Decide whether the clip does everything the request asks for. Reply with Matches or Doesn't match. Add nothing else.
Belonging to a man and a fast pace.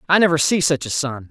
Matches